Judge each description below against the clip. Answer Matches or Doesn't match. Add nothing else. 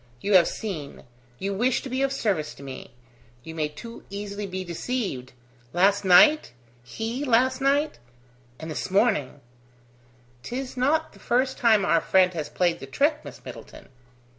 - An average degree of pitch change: Doesn't match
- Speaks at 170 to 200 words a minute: Doesn't match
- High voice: Matches